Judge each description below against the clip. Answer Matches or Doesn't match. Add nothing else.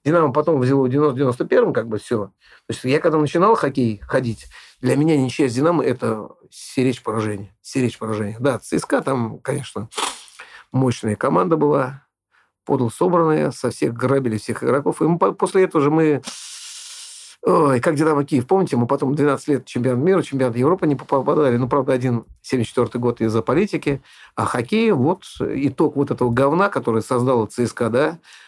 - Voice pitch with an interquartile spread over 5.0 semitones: Doesn't match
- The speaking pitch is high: Doesn't match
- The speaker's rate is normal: Doesn't match